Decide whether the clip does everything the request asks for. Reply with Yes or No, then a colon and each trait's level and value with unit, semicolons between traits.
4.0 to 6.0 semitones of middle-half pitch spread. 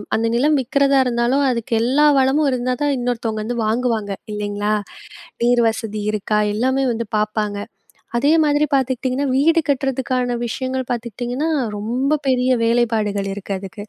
No: average, 3.3 semitones